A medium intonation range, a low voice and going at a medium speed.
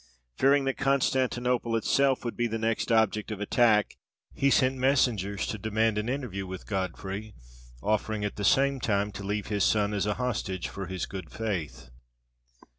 Yes: average, 3.8 semitones; low, 110 Hz; average, 170 wpm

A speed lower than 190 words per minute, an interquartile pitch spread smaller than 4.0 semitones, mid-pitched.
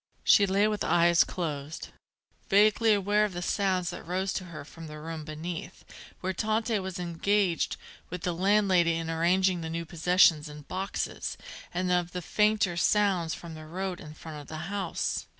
Yes: average, 175 wpm; average, 3.0 semitones; medium, 180 Hz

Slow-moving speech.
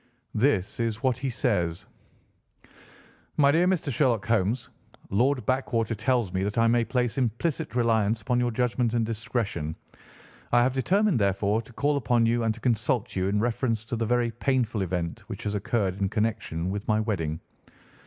No: average, 170 wpm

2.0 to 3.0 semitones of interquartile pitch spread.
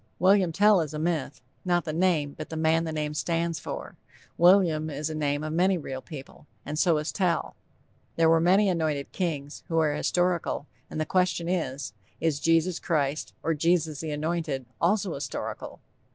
Yes: narrow, 2.6 semitones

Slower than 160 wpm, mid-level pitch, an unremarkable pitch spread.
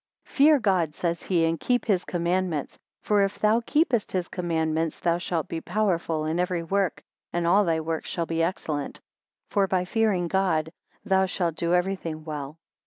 No: average, 175 wpm; medium, 175 Hz; average, 3.0 semitones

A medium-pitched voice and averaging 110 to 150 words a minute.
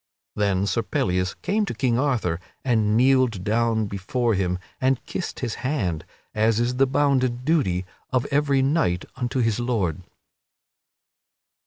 No: low, 120 Hz; average, 140 wpm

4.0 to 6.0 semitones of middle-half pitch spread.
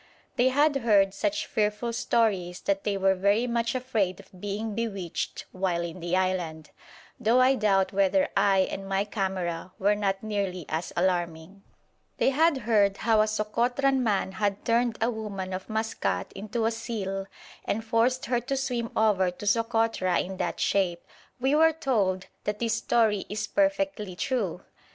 No: average, 3.6 semitones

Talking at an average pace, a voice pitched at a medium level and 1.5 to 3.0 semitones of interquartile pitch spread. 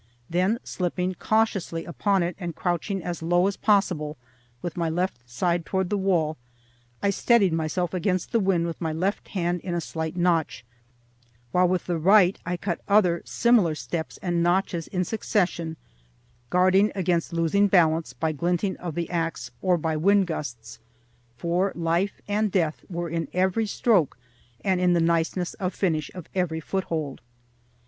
Yes: average, 160 wpm; medium, 175 Hz; narrow, 2.5 semitones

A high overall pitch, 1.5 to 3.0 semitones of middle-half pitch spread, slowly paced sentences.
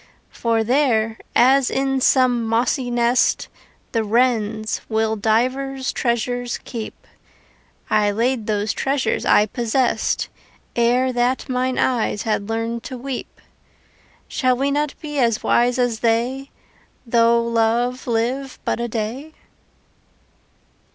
Yes: high, 240 Hz; narrow, 2.4 semitones; slow, 115 wpm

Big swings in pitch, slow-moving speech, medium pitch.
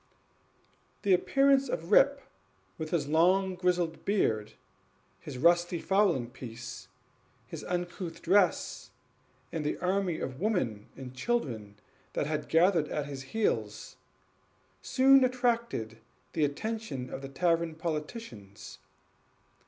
Yes: wide, 6.9 semitones; slow, 105 wpm; medium, 165 Hz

